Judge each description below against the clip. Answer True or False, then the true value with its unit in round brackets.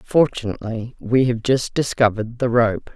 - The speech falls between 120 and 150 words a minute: True (140 wpm)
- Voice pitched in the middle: False (120 Hz)